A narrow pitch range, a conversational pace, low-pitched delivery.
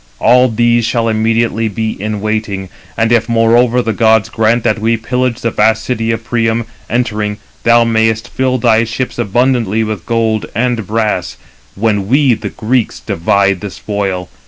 Yes: narrow, 1.6 semitones; average, 160 wpm; low, 115 Hz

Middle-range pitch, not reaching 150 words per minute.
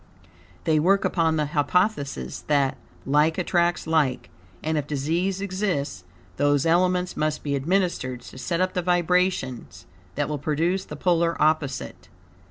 Yes: medium, 160 Hz; average, 140 wpm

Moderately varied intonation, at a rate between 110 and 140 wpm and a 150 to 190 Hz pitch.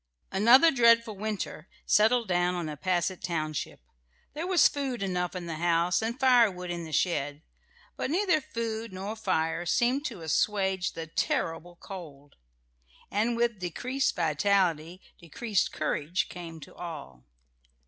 No: wide, 5.7 semitones; slow, 135 wpm; medium, 185 Hz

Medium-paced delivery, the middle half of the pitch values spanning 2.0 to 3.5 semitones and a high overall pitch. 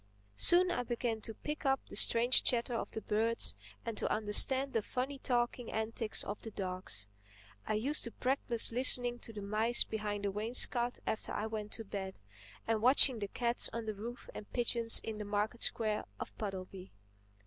Yes: average, 180 wpm; narrow, 2.5 semitones; high, 225 Hz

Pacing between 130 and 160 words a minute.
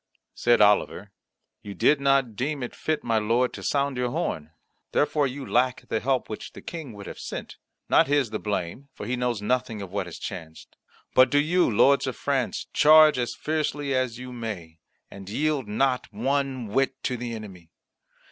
No: average, 185 wpm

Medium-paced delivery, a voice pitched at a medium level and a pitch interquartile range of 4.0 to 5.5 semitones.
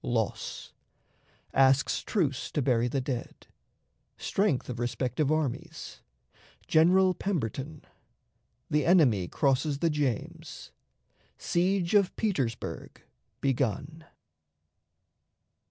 No: slow, 85 wpm; medium, 145 Hz; average, 5.1 semitones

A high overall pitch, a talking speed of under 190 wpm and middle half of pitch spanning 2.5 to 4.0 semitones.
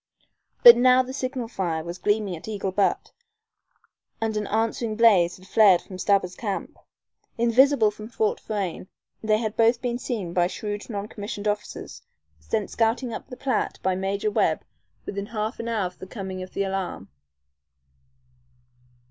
Yes: high, 210 Hz; average, 160 wpm; average, 3.1 semitones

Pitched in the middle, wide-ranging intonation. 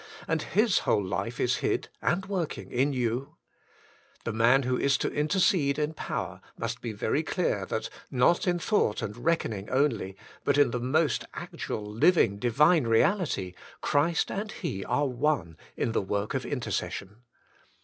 No: low, 130 Hz; wide, 6.1 semitones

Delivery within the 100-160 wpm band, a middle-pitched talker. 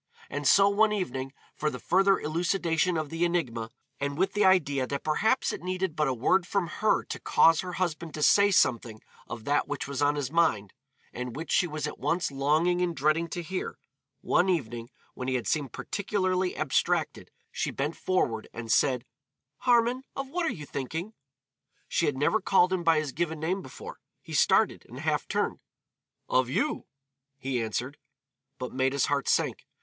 No: average, 185 wpm; medium, 155 Hz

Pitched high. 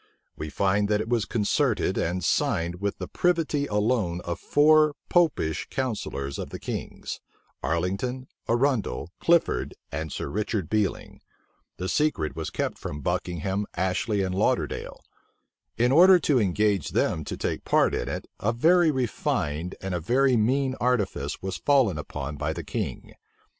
No: low, 105 Hz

